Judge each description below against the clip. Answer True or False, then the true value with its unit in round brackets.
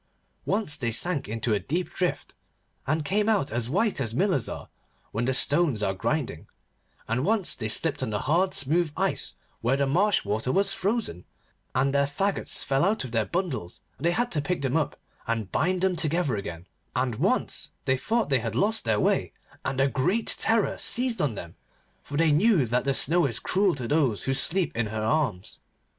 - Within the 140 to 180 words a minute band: False (200 wpm)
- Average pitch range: False (7.5 semitones)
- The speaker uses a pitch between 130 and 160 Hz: True (140 Hz)